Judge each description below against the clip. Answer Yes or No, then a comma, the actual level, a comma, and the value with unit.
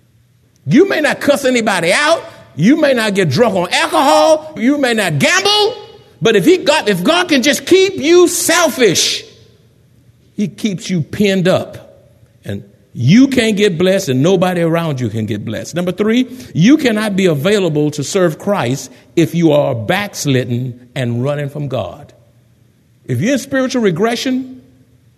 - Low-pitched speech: No, medium, 185 Hz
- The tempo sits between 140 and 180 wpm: Yes, average, 160 wpm